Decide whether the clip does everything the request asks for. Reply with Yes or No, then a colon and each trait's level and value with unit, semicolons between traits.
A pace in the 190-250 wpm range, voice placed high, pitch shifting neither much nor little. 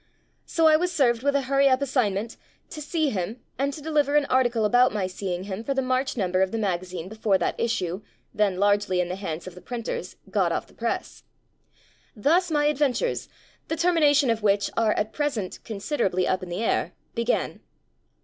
No: average, 195 wpm; high, 230 Hz; wide, 6.5 semitones